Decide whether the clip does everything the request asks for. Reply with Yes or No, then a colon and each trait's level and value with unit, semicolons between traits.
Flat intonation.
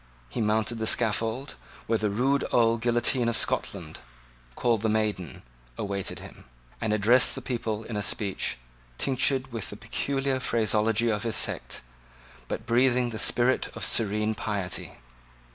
Yes: narrow, 2.3 semitones